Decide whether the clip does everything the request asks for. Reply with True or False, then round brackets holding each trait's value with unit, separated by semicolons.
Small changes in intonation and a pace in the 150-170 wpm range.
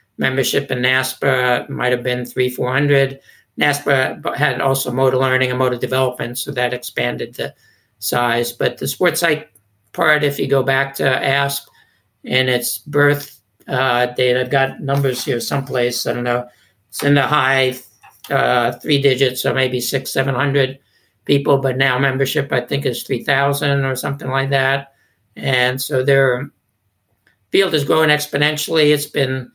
True (1.9 semitones; 160 wpm)